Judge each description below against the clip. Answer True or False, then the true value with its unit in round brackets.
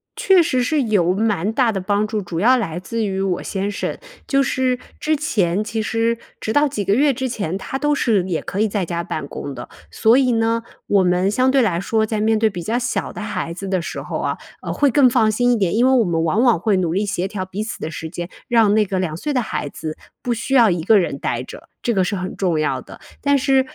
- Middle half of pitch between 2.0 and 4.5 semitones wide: False (4.9 semitones)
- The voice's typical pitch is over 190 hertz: True (215 Hz)